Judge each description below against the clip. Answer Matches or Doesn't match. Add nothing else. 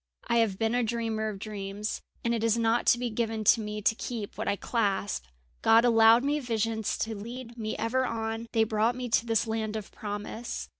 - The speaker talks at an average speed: Doesn't match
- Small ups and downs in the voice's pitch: Matches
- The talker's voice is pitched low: Doesn't match